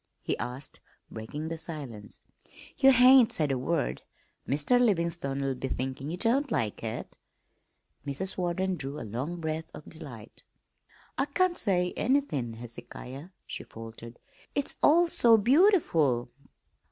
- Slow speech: Yes, slow, 130 wpm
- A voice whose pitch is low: No, medium, 155 Hz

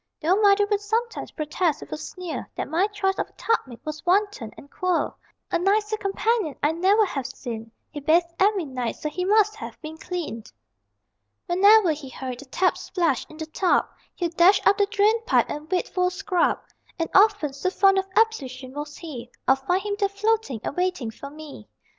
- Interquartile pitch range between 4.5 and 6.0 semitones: Yes, wide, 5.4 semitones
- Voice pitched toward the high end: Yes, very high, 360 Hz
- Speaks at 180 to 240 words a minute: Yes, average, 200 wpm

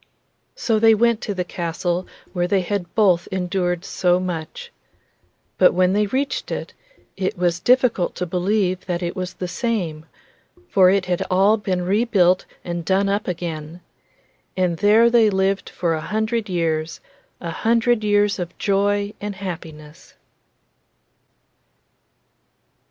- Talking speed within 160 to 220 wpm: No, average, 140 wpm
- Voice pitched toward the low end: No, medium, 185 Hz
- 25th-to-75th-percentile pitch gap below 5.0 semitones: Yes, average, 2.8 semitones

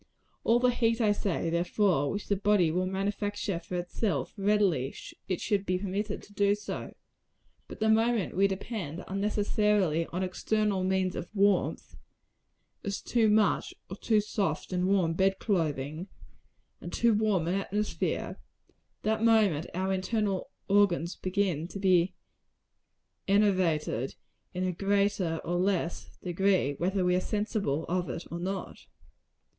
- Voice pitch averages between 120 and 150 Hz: No, high, 195 Hz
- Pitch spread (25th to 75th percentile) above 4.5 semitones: No, average, 2.7 semitones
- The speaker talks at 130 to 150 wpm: Yes, average, 140 wpm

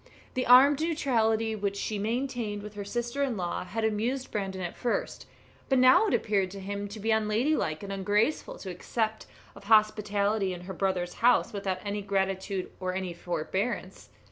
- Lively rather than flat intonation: No, average, 3.2 semitones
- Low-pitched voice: No, high, 210 Hz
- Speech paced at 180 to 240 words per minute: No, average, 170 wpm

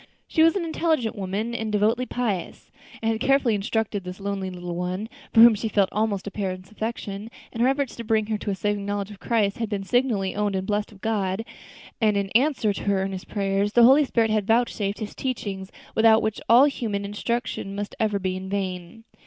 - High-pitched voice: Yes, high, 210 Hz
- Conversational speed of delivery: No, fast, 210 wpm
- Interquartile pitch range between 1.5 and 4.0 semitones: Yes, average, 2.7 semitones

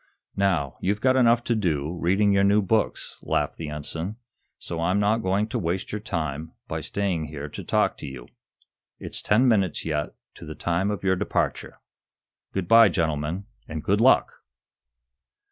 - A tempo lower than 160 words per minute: No, average, 170 wpm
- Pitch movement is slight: No, average, 4.6 semitones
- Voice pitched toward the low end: Yes, very low, 95 Hz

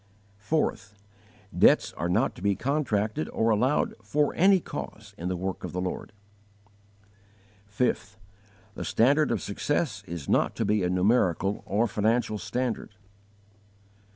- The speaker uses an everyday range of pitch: Yes, average, 4.6 semitones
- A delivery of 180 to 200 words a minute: No, slow, 135 wpm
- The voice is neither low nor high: No, low, 105 Hz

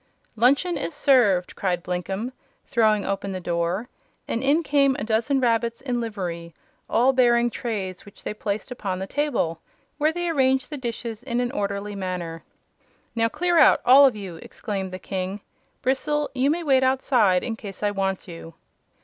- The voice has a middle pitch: No, high, 230 Hz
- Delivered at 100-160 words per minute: No, average, 170 wpm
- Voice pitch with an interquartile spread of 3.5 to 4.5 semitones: No, wide, 5.5 semitones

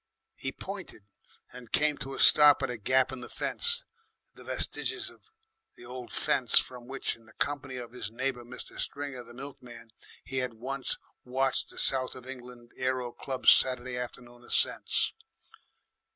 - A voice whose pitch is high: No, low, 125 Hz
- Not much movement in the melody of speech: Yes, narrow, 1.7 semitones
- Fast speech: No, average, 165 wpm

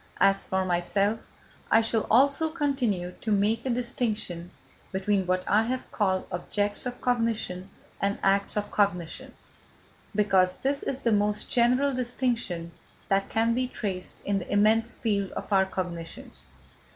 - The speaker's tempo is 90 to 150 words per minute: Yes, average, 145 wpm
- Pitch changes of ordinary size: Yes, average, 3.9 semitones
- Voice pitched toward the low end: No, high, 205 Hz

